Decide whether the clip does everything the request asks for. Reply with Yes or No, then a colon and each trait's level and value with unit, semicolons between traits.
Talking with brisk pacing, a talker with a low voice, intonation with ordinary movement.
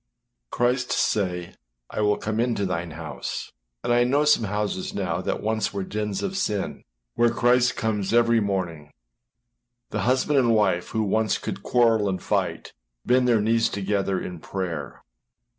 No: average, 160 wpm; low, 105 Hz; average, 3.8 semitones